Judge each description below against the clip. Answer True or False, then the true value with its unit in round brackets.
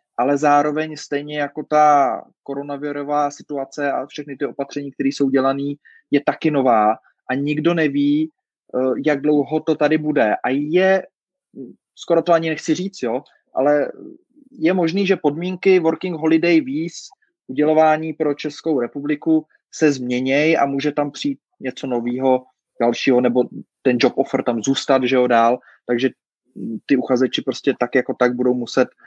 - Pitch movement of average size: True (3.0 semitones)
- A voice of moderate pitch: True (145 Hz)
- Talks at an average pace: True (150 wpm)